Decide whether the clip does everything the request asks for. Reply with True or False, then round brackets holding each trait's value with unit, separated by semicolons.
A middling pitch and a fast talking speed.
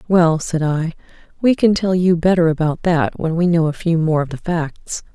True (165 Hz; 220 wpm)